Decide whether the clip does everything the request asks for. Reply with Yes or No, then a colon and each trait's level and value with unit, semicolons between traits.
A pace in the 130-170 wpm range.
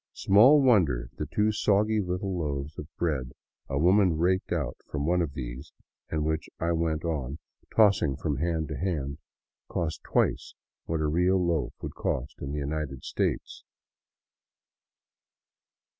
Yes: average, 145 wpm